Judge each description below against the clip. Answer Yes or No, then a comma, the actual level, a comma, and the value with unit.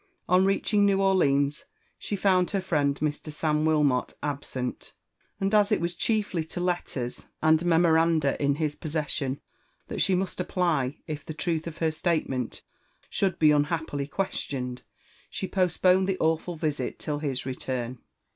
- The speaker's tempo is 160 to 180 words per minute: No, average, 150 wpm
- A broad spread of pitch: No, average, 4.1 semitones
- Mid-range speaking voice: Yes, medium, 160 Hz